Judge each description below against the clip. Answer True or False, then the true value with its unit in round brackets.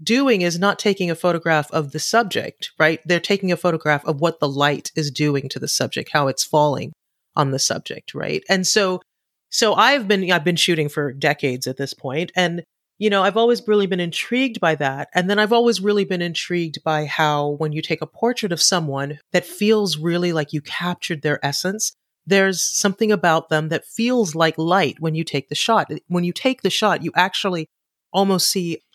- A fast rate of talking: True (210 wpm)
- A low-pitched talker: False (175 Hz)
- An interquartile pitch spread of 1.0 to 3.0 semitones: False (4.2 semitones)